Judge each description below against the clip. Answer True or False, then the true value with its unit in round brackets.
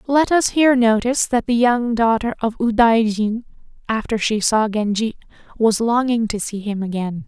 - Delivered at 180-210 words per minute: False (165 wpm)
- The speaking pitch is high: True (225 Hz)